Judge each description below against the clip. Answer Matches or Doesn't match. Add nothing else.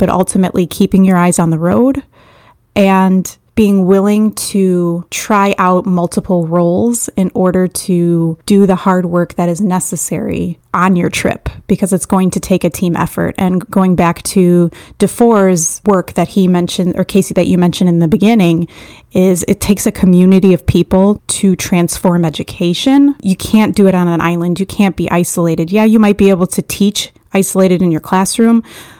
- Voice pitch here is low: Doesn't match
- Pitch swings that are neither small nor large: Doesn't match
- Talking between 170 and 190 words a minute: Matches